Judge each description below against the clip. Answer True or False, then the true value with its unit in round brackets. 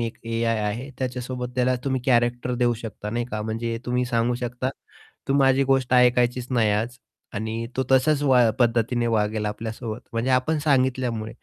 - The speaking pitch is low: True (120 Hz)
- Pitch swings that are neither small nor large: False (1.9 semitones)